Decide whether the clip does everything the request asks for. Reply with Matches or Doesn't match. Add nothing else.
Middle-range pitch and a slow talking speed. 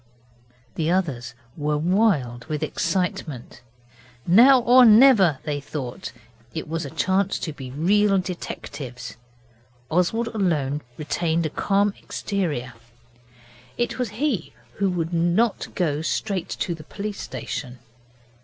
Matches